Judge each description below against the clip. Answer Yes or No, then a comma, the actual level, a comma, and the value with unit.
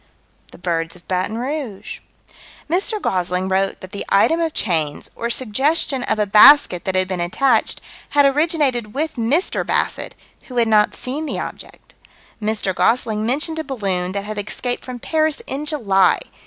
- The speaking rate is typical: Yes, average, 165 wpm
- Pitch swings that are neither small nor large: No, wide, 7.1 semitones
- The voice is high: Yes, high, 225 Hz